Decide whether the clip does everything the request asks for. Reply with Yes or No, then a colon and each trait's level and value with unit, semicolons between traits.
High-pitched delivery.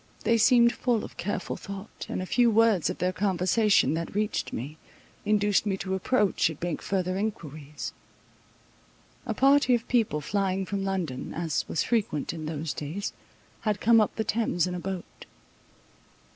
Yes: high, 195 Hz